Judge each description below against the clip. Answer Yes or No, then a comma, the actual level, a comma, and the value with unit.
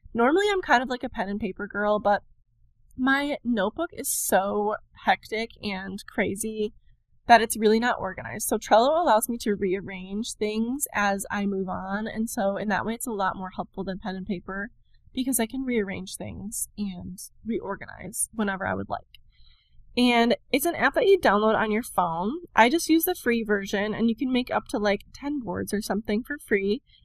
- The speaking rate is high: No, average, 195 wpm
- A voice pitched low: No, high, 215 Hz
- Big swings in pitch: No, average, 3.4 semitones